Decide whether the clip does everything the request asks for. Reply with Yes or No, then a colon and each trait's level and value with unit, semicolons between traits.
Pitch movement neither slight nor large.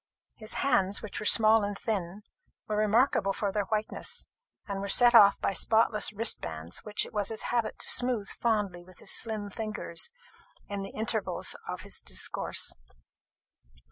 No: narrow, 2.0 semitones